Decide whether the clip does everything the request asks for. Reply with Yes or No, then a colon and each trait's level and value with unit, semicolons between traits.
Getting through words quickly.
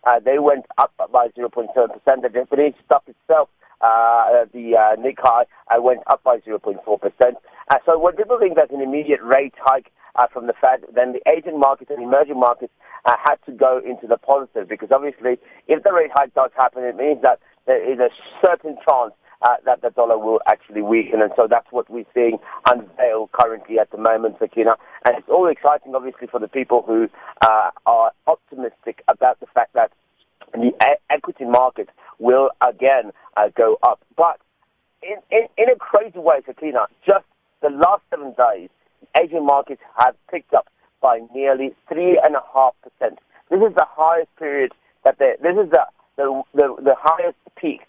No: average, 185 wpm